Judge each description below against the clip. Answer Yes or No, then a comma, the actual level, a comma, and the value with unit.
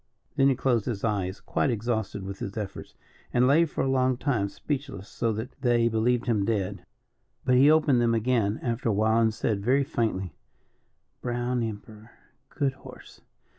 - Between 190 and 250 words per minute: No, average, 170 wpm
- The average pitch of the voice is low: Yes, low, 115 Hz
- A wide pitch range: No, average, 3.2 semitones